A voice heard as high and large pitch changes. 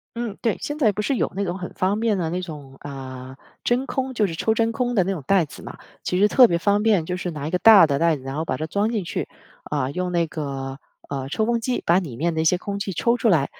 No: medium, 180 Hz; wide, 5.9 semitones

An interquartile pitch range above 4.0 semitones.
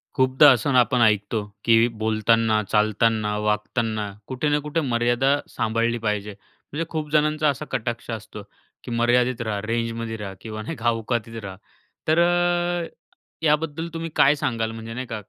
Yes: average, 4.6 semitones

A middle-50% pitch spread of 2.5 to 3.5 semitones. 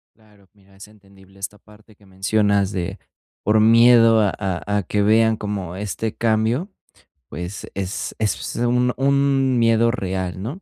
Yes: average, 2.8 semitones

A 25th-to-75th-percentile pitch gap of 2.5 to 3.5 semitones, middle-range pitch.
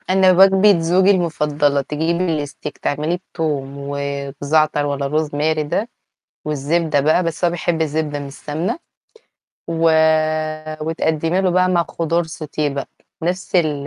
Yes: average, 3.0 semitones; medium, 155 Hz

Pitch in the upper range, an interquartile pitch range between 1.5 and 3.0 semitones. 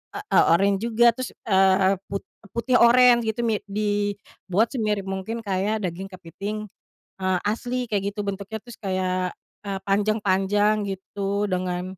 Yes: high, 200 Hz; narrow, 2.6 semitones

